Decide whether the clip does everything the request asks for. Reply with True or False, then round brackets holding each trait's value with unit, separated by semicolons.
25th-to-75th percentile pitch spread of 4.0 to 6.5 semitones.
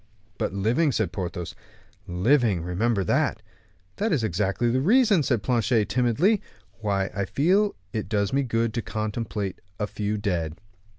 True (4.8 semitones)